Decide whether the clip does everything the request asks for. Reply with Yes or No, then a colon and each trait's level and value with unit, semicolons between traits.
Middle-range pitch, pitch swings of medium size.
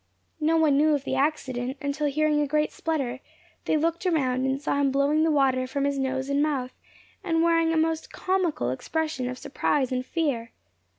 No: very high, 285 Hz; average, 3.1 semitones